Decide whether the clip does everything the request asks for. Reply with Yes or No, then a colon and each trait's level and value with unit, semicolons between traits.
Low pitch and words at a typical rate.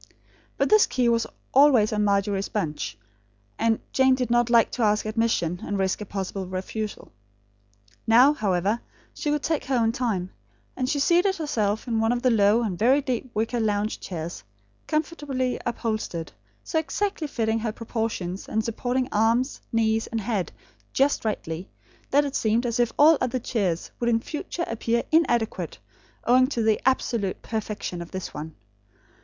No: high, 230 Hz; average, 165 wpm